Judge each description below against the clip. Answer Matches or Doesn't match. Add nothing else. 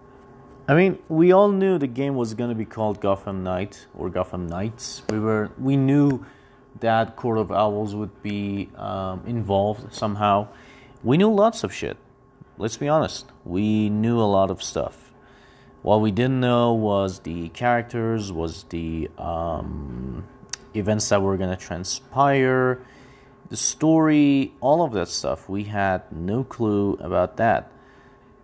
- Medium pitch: Doesn't match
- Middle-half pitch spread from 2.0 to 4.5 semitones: Doesn't match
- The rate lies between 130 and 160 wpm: Matches